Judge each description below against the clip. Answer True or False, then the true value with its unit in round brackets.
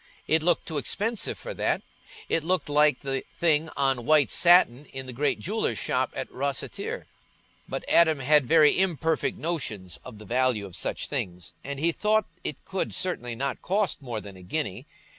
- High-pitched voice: False (150 Hz)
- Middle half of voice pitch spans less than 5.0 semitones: False (5.3 semitones)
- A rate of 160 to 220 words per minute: True (175 wpm)